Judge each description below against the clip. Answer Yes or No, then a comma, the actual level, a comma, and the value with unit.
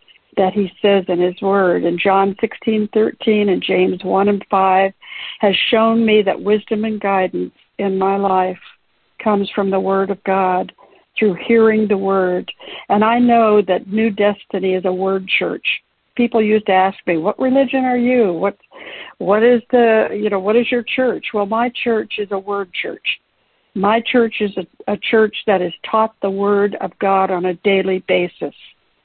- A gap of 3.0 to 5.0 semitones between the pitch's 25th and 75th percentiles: No, narrow, 2.5 semitones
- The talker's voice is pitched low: No, high, 205 Hz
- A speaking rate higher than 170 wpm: Yes, average, 180 wpm